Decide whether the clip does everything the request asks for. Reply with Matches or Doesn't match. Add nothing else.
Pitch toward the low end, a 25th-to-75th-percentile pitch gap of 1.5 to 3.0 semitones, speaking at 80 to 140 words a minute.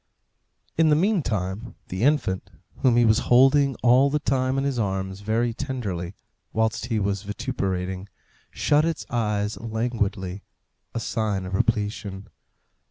Doesn't match